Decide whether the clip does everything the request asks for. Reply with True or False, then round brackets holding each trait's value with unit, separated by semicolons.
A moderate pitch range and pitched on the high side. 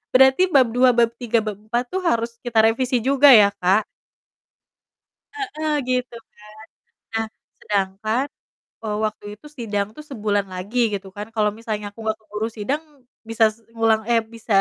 True (3.1 semitones; 225 Hz)